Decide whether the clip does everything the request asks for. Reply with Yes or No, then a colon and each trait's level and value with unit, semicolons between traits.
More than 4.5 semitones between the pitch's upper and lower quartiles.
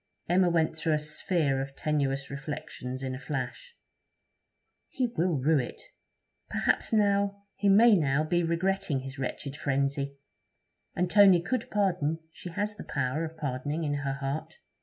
Yes: average, 5.2 semitones